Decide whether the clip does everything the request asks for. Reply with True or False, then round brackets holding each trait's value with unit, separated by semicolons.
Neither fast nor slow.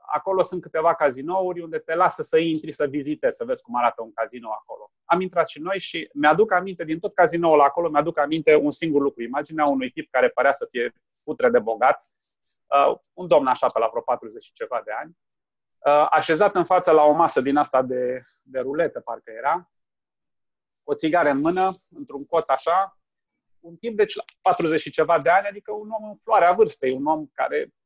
False (200 wpm)